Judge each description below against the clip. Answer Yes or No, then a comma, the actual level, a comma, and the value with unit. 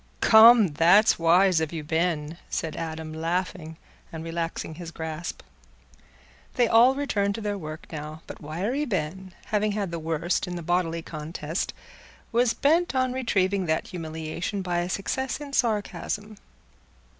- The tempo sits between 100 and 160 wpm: Yes, average, 145 wpm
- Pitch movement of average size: Yes, average, 4.7 semitones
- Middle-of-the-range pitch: Yes, medium, 175 Hz